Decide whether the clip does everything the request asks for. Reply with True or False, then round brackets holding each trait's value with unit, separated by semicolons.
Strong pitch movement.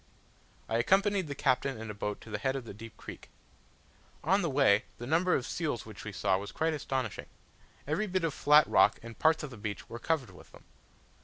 True (6.5 semitones)